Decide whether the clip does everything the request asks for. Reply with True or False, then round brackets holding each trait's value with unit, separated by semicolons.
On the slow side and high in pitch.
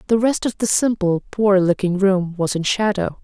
False (205 wpm; 195 Hz)